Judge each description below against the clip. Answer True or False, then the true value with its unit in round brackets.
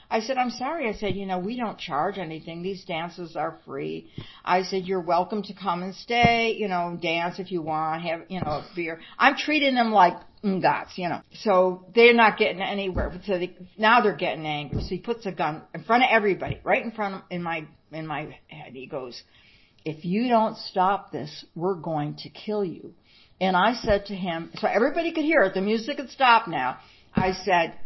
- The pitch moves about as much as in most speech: True (4.5 semitones)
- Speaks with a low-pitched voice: False (185 Hz)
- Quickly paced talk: True (215 wpm)